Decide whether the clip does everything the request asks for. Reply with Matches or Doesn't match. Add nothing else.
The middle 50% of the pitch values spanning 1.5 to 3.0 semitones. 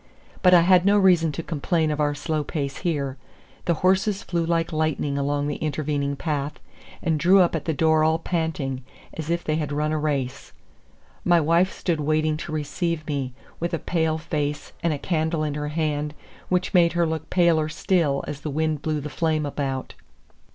Matches